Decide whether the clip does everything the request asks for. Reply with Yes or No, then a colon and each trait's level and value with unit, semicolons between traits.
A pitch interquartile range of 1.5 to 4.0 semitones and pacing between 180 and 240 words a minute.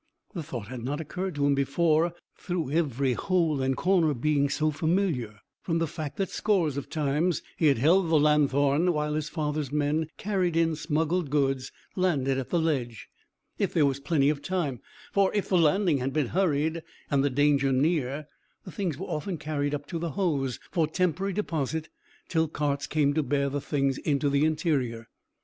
Yes: average, 3.1 semitones; average, 185 wpm